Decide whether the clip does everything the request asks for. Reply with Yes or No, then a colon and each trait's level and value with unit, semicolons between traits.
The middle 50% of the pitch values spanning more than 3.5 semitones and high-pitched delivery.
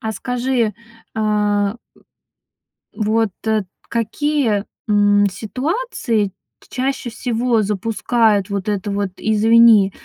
No: narrow, 2.5 semitones; high, 220 Hz